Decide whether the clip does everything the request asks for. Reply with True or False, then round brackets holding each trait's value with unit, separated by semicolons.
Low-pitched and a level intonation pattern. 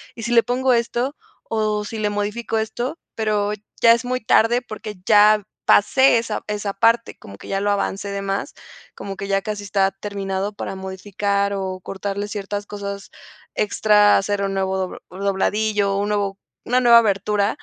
False (205 Hz; 1.9 semitones)